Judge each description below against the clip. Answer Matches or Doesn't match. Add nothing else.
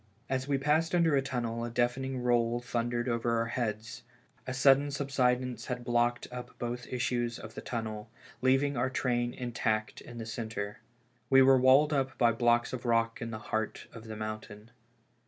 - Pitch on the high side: Doesn't match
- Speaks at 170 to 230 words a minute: Matches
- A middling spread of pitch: Doesn't match